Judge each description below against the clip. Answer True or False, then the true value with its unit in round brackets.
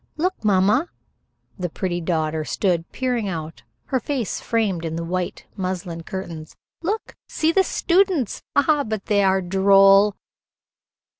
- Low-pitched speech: False (195 Hz)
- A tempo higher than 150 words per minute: False (135 wpm)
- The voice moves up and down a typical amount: False (6.4 semitones)